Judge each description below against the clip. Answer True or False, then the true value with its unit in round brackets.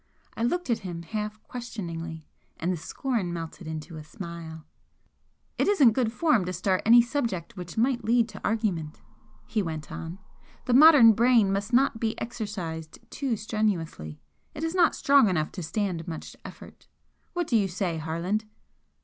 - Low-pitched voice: False (205 Hz)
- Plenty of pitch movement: True (6.1 semitones)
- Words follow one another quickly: False (165 wpm)